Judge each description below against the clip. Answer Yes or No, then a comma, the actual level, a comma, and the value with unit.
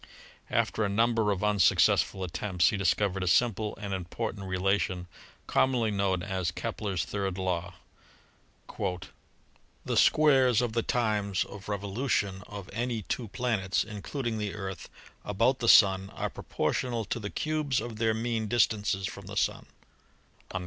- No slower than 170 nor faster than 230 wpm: No, average, 150 wpm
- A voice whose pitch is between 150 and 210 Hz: No, low, 105 Hz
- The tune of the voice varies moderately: Yes, average, 3.1 semitones